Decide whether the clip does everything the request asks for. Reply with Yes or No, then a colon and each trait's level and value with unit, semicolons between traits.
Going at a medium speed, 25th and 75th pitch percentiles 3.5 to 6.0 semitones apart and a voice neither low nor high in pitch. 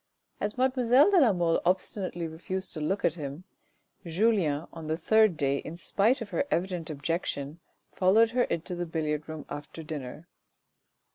Yes: average, 160 wpm; average, 5.0 semitones; medium, 170 Hz